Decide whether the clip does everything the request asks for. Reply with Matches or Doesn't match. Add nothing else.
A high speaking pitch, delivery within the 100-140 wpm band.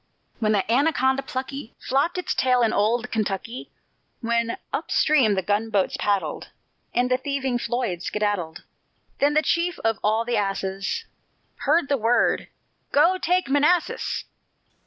Matches